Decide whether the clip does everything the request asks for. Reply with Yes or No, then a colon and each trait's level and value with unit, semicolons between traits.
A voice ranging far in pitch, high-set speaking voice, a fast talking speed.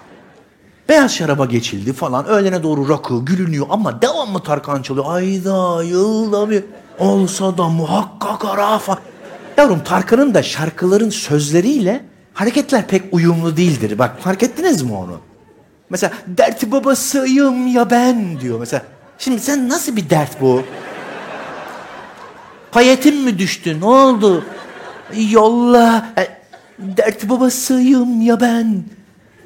No: wide, 6.2 semitones; high, 200 Hz; average, 120 wpm